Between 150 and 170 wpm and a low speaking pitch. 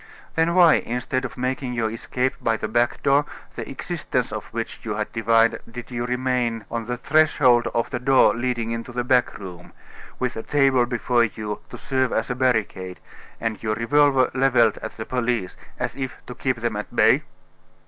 No: average, 190 wpm; low, 120 Hz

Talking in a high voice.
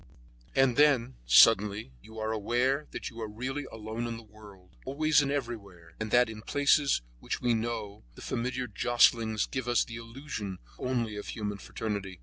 No: low, 115 Hz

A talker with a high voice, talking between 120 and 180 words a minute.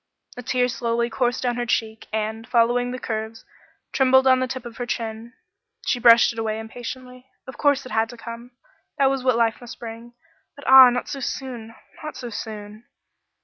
No: high, 240 Hz; average, 190 wpm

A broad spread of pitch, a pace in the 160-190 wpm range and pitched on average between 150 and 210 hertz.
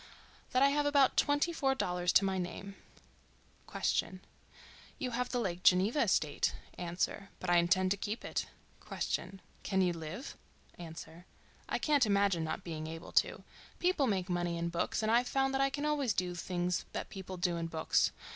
Yes: wide, 6.5 semitones; average, 170 wpm; high, 190 Hz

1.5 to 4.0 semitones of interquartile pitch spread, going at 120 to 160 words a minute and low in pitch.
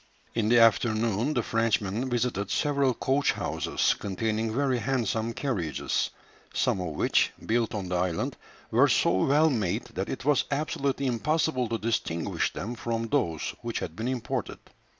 Yes: average, 3.7 semitones; average, 150 wpm; low, 115 Hz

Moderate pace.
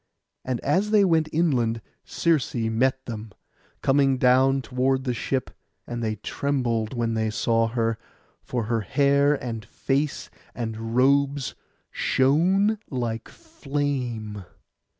No: slow, 120 wpm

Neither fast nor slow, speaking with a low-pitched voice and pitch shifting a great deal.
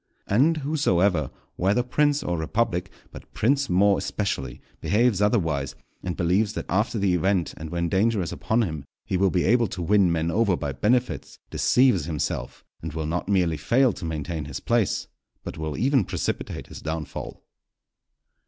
Yes: average, 165 wpm; very low, 95 Hz; wide, 5.9 semitones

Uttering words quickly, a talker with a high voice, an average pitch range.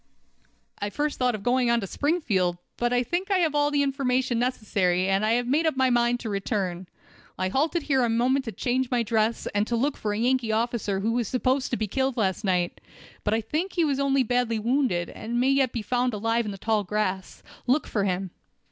Yes: fast, 230 wpm; high, 240 Hz; average, 4.0 semitones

